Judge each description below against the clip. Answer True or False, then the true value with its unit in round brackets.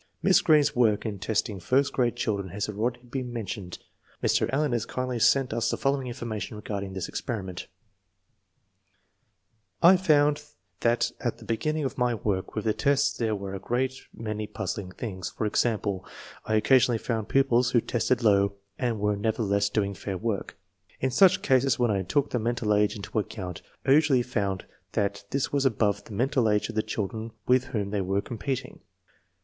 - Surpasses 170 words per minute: True (185 wpm)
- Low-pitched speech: True (115 Hz)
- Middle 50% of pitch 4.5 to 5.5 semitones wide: False (3.9 semitones)